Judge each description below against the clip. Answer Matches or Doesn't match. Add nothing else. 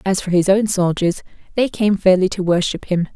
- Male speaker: Doesn't match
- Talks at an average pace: Doesn't match